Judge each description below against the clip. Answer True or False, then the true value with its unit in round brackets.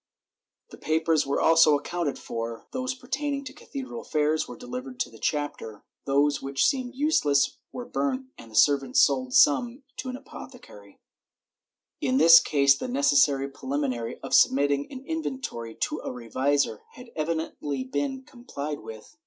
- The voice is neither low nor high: True (150 Hz)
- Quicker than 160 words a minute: False (155 wpm)